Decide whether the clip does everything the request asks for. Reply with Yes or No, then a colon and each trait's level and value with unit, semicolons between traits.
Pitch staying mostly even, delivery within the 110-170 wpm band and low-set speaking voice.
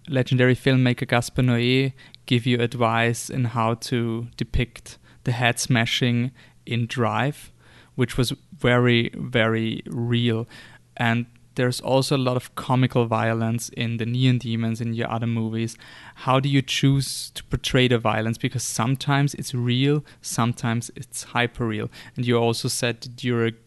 Yes: narrow, 1.7 semitones; average, 150 wpm; low, 120 Hz